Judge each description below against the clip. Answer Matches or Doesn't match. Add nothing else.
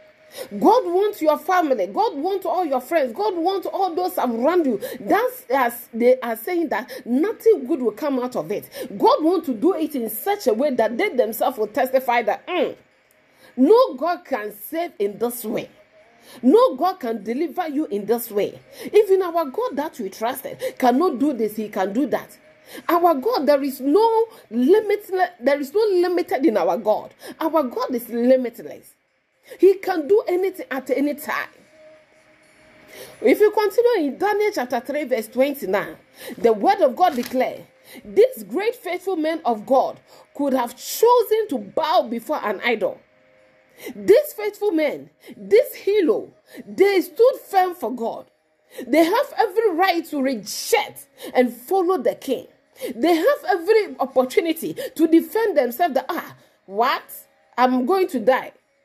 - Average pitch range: Doesn't match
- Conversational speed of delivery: Matches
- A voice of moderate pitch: Doesn't match